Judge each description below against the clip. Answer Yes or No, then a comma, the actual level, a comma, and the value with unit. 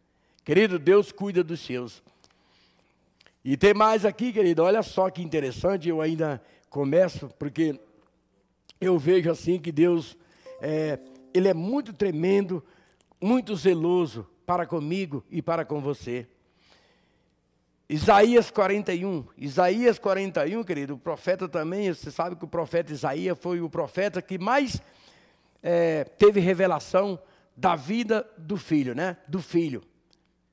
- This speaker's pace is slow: No, average, 130 wpm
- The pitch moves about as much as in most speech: Yes, average, 3.5 semitones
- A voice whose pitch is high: No, medium, 175 Hz